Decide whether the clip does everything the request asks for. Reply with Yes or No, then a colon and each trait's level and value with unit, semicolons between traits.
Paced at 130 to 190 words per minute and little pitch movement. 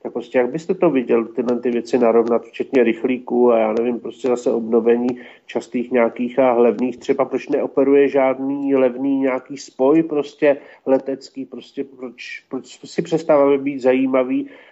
Yes: average, 155 wpm; narrow, 2.2 semitones